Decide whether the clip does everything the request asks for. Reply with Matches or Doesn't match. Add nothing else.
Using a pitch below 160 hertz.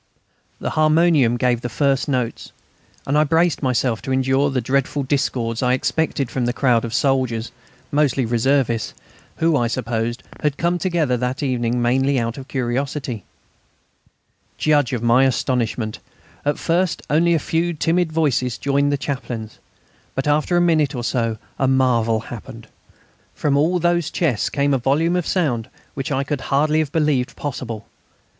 Matches